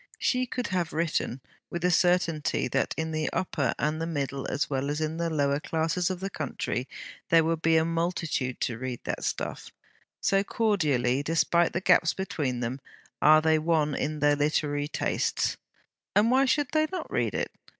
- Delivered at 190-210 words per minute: No, average, 180 wpm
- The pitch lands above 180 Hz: No, medium, 160 Hz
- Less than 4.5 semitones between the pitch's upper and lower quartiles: Yes, average, 3.3 semitones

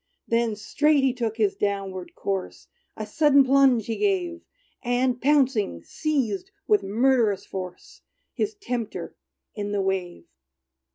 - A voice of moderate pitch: No, high, 235 Hz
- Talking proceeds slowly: Yes, slow, 125 wpm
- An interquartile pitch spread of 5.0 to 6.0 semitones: Yes, wide, 5.5 semitones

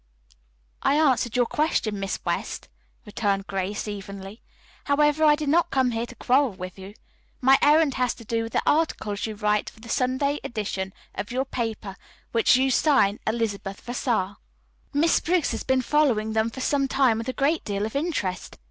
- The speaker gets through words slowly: No, average, 180 wpm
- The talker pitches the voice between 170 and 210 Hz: No, high, 235 Hz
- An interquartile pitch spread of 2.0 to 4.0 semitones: No, average, 5.2 semitones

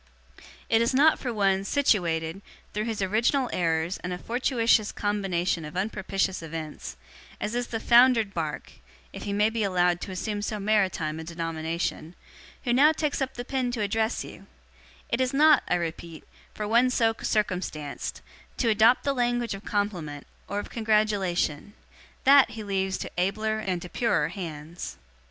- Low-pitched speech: No, high, 205 Hz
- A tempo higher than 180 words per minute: No, average, 165 wpm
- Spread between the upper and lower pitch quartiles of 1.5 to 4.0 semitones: No, average, 4.8 semitones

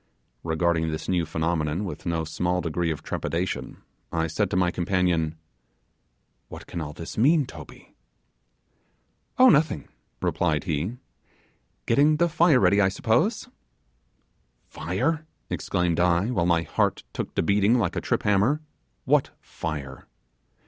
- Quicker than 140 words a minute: No, slow, 135 wpm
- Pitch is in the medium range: No, very low, 90 Hz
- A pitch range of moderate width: Yes, average, 4.2 semitones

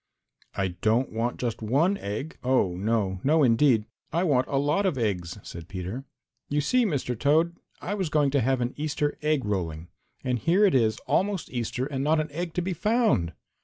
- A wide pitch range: Yes, wide, 6.3 semitones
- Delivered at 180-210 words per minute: Yes, average, 195 wpm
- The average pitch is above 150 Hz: No, low, 135 Hz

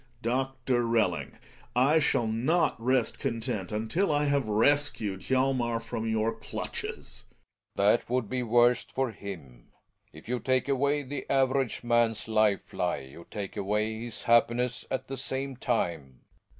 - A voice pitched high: No, low, 120 Hz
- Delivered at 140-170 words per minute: Yes, average, 145 wpm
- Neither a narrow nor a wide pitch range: Yes, average, 3.5 semitones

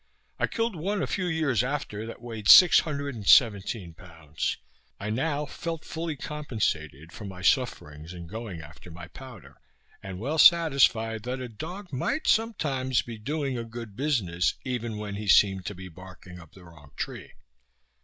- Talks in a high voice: No, low, 115 Hz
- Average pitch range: No, wide, 7.6 semitones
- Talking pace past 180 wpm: No, average, 170 wpm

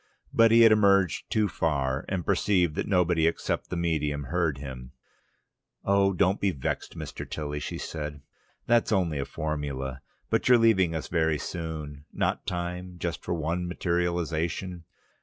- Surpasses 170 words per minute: No, average, 155 wpm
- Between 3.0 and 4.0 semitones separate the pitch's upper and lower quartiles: Yes, average, 3.7 semitones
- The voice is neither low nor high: No, very low, 85 Hz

